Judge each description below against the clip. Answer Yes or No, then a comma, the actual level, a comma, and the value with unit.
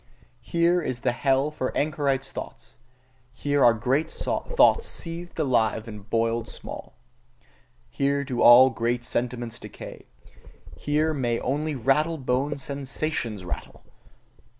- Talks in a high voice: No, low, 135 Hz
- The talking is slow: Yes, slow, 120 wpm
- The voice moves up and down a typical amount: Yes, average, 4.0 semitones